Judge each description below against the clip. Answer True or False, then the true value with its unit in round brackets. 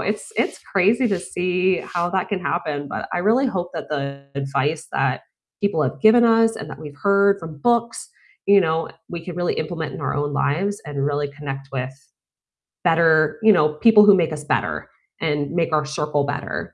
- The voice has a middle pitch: True (165 Hz)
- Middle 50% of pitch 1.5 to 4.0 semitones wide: False (5.2 semitones)